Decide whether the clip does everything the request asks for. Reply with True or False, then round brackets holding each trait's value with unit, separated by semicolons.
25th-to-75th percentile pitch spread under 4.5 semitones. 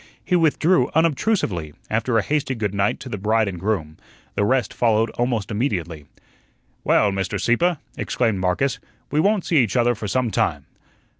False (5.2 semitones)